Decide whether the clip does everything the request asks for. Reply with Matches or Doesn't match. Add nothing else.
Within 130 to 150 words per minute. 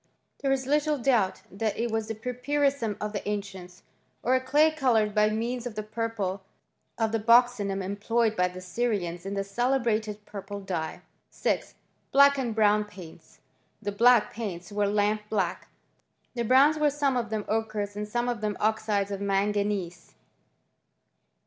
Doesn't match